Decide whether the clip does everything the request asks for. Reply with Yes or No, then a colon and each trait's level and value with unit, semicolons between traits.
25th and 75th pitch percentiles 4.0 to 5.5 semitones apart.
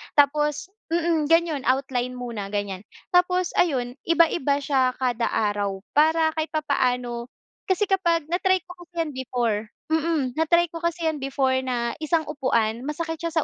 Yes: average, 5.1 semitones